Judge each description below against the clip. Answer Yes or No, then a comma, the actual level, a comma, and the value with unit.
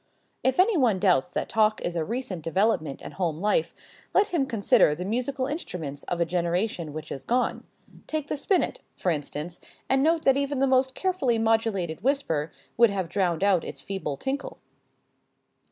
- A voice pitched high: Yes, high, 205 Hz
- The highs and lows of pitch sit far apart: Yes, wide, 7.7 semitones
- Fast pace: No, average, 175 wpm